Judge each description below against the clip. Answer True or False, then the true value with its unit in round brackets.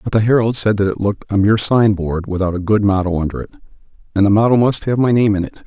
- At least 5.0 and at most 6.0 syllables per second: False (6.6 syllables/s)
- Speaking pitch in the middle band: False (105 Hz)